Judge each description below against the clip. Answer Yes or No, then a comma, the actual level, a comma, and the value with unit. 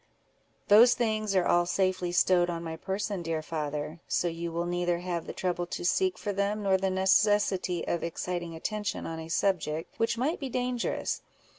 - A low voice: No, medium, 180 Hz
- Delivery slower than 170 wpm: No, average, 180 wpm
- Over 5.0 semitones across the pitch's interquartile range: No, average, 3.4 semitones